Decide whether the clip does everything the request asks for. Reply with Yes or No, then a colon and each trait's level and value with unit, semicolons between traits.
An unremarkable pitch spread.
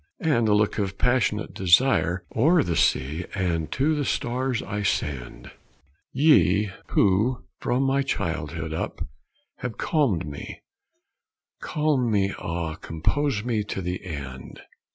No: wide, 7.5 semitones